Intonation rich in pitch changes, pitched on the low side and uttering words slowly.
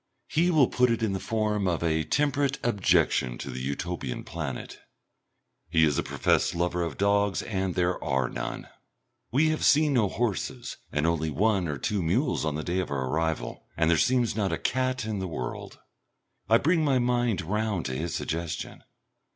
No: wide, 7.0 semitones; very low, 95 Hz; average, 185 wpm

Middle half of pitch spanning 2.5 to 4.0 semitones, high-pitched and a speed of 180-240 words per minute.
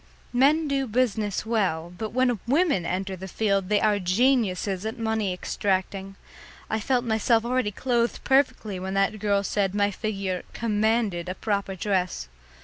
No: average, 3.5 semitones; high, 210 Hz; average, 150 wpm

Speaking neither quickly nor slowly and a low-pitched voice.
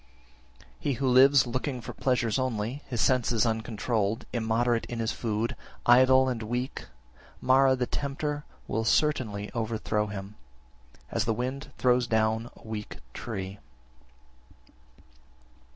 No: slow, 125 wpm; low, 120 Hz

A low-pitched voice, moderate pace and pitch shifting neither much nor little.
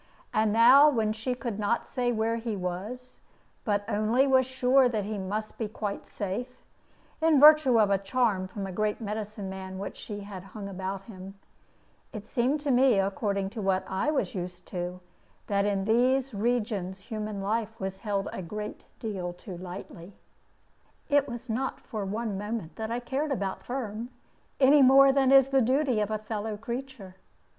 No: high, 215 Hz; average, 175 wpm; average, 4.2 semitones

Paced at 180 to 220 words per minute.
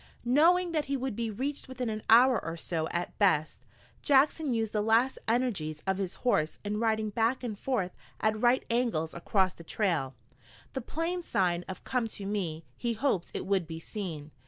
Yes: average, 185 wpm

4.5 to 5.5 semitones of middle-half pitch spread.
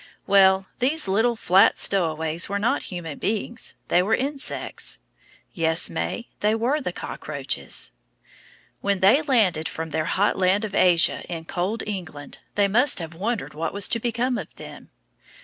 Yes: average, 5.0 semitones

